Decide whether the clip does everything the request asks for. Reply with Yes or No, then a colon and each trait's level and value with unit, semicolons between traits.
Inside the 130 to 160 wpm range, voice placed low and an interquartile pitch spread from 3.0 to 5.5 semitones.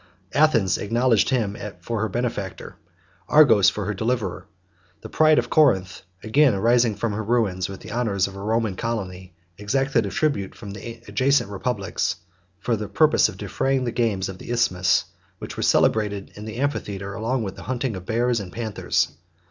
No: average, 175 wpm; low, 110 Hz; average, 3.6 semitones